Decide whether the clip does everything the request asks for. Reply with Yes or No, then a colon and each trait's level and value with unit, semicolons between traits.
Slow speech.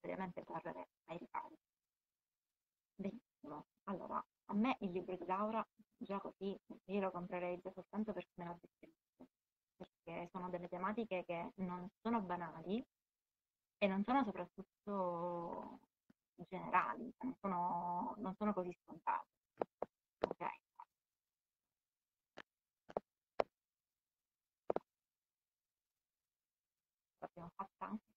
Yes: slow, 90 wpm